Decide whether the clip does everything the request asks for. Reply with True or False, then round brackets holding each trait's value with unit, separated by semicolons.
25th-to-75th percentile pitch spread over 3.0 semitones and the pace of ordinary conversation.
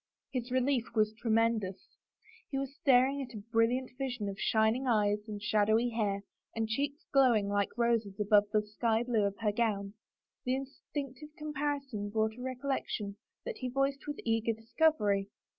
True (4.0 semitones; 165 wpm)